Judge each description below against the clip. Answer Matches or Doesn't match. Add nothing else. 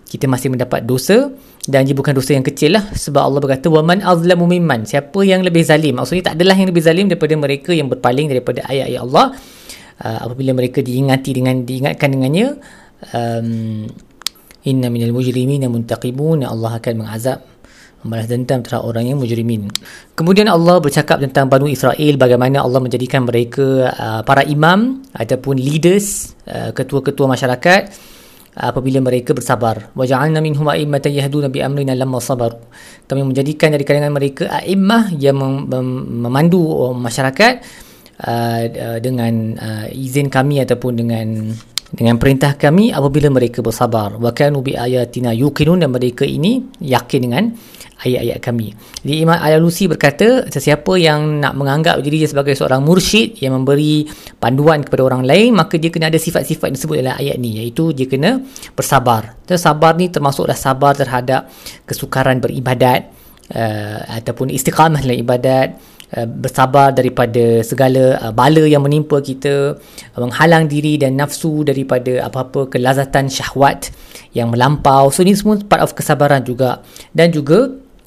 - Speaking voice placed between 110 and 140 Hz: Matches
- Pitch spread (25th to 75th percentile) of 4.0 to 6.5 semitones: Doesn't match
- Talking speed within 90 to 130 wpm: Doesn't match